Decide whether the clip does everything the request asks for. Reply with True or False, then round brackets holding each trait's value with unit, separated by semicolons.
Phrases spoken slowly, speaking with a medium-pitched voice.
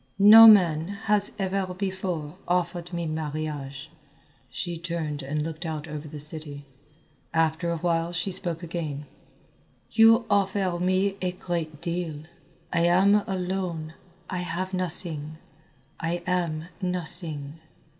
True (125 wpm; 170 Hz)